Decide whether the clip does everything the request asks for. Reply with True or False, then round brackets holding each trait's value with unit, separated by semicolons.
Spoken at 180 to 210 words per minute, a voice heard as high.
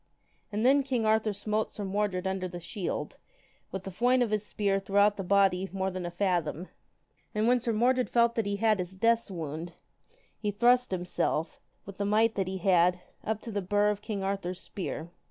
True (200 wpm; 200 Hz)